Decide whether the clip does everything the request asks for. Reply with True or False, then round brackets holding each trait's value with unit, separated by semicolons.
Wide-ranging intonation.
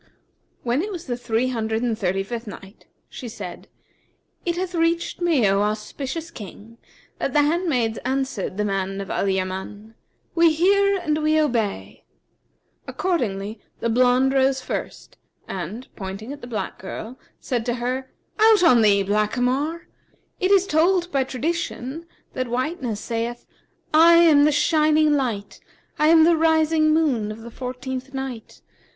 True (6.2 semitones)